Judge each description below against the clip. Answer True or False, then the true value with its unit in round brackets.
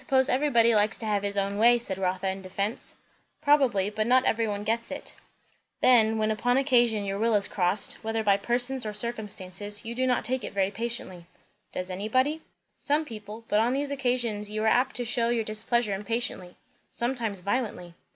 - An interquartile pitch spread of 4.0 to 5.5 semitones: False (3.2 semitones)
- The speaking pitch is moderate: False (220 Hz)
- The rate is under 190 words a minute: False (200 wpm)